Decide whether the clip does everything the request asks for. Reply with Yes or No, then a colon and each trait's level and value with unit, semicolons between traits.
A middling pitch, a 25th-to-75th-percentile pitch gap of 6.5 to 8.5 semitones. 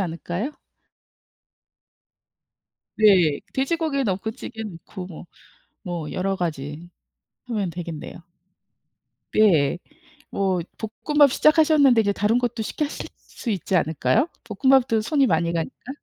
No: high, 205 Hz; wide, 6.9 semitones